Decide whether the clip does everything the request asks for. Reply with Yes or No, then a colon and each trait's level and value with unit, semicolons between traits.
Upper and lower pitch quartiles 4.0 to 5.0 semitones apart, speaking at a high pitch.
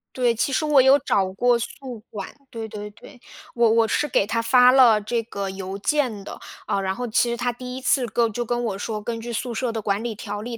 No: average, 2.9 semitones; high, 230 Hz